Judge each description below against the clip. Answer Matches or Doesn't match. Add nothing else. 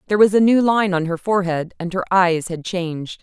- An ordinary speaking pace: Doesn't match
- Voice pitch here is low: Doesn't match